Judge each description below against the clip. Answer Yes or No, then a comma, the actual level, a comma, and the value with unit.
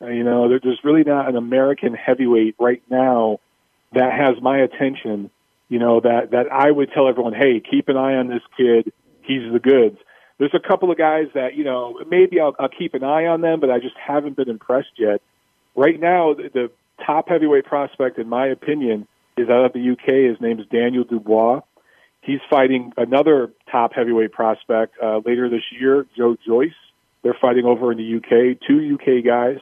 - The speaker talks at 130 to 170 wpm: No, average, 195 wpm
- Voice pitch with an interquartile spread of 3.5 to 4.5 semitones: No, average, 2.8 semitones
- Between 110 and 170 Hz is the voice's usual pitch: Yes, low, 125 Hz